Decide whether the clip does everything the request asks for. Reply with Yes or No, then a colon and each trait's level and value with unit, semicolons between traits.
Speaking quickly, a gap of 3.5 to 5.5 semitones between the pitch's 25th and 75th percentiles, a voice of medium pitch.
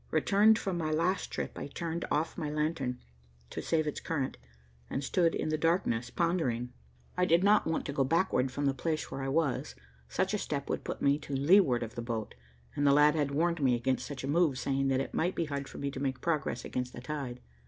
Yes: fast, 230 wpm; average, 3.8 semitones; medium, 145 Hz